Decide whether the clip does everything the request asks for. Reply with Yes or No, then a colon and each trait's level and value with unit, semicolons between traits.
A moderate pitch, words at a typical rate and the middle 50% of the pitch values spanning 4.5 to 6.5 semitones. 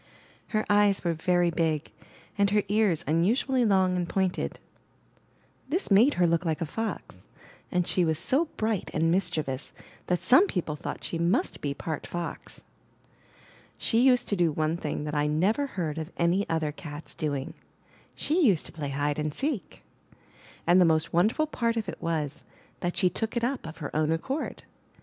Yes: medium, 175 Hz; average, 175 wpm; average, 5.1 semitones